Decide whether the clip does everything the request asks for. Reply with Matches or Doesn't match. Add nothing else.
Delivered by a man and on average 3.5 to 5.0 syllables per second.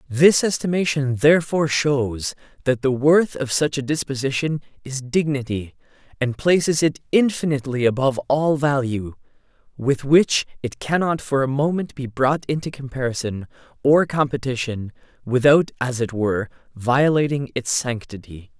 Matches